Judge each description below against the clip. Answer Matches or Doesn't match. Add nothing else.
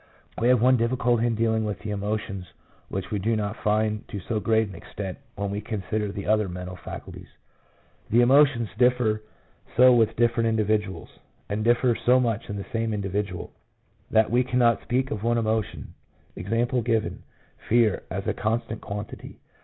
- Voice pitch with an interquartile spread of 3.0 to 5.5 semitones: Doesn't match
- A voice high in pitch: Doesn't match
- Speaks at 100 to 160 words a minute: Doesn't match